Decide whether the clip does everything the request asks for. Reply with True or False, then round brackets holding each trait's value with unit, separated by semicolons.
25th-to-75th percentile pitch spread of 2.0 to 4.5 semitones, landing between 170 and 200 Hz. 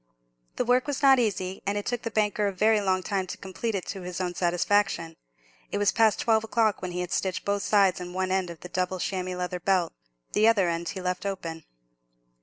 True (2.7 semitones; 190 Hz)